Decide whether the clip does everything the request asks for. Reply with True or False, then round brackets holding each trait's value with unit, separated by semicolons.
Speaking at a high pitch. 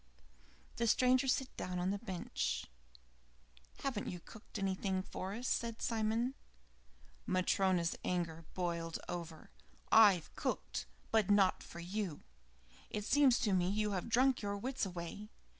True (200 Hz)